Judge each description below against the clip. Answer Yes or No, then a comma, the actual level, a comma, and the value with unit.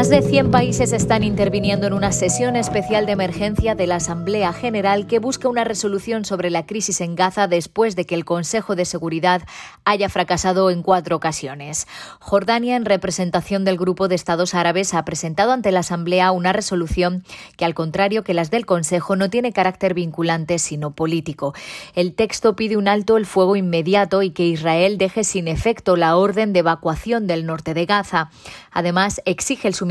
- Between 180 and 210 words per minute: Yes, average, 185 wpm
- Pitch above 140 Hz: Yes, medium, 185 Hz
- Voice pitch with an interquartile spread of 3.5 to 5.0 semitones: No, average, 2.9 semitones